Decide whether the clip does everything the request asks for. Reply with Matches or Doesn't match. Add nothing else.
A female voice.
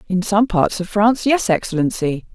Matches